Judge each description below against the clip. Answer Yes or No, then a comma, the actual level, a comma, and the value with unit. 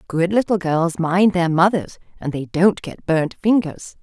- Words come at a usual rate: Yes, average, 180 wpm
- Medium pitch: Yes, medium, 180 Hz